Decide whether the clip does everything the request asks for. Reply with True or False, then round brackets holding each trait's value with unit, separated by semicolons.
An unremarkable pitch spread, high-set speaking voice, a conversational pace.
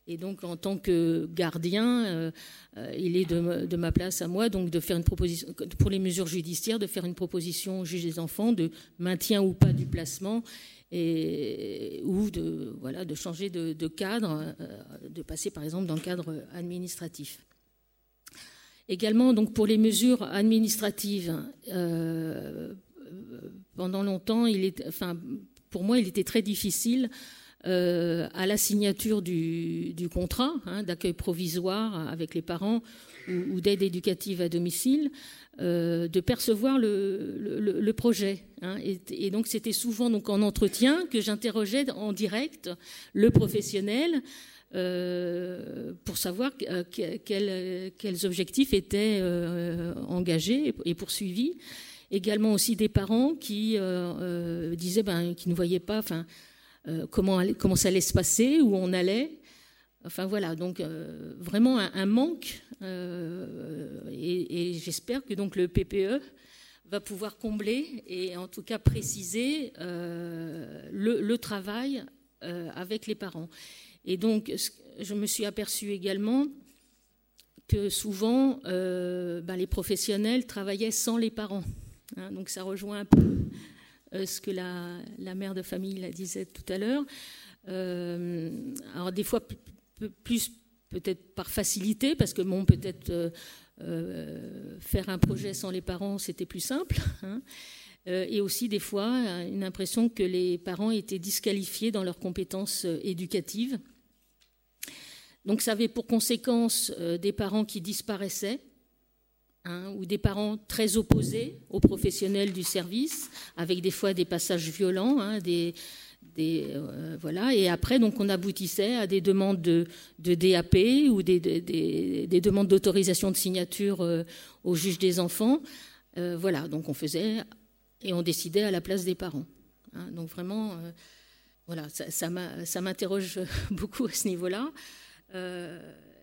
True (3.8 semitones; 195 Hz; 155 wpm)